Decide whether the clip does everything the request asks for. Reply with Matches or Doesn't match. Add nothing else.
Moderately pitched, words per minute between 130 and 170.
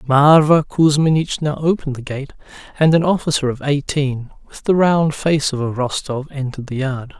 Matches